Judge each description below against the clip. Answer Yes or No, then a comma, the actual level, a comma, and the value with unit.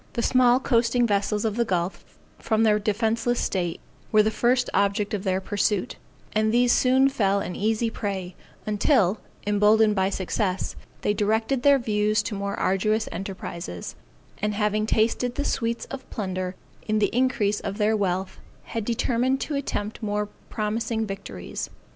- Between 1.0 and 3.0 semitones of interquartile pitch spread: Yes, narrow, 2.6 semitones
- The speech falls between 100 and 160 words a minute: Yes, average, 155 wpm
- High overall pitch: Yes, high, 215 Hz